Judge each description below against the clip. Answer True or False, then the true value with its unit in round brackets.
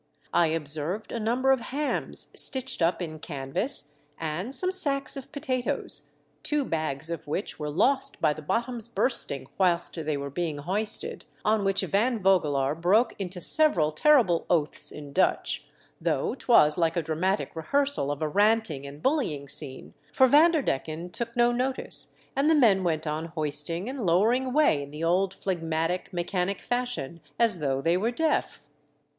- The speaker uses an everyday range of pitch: False (7.8 semitones)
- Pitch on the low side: False (180 Hz)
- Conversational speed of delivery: True (160 wpm)